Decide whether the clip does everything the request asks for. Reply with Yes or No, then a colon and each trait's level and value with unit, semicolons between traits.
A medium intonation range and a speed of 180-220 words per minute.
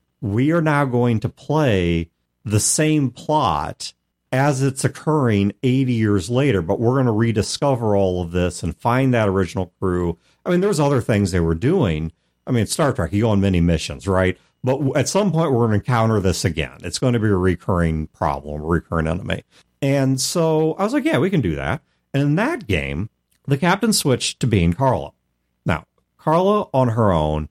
No: wide, 8.1 semitones; average, 200 wpm